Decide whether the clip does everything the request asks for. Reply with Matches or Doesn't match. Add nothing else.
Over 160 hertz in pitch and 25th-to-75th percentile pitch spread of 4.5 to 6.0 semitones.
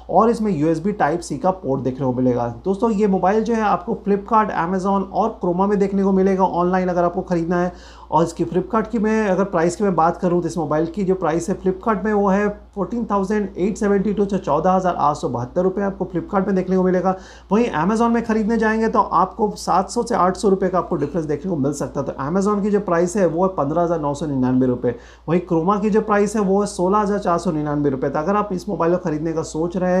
Doesn't match